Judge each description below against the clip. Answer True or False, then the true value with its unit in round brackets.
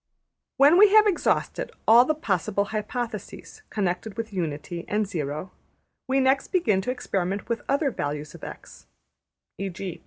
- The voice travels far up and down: True (6.5 semitones)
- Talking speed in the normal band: True (145 wpm)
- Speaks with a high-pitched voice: True (210 Hz)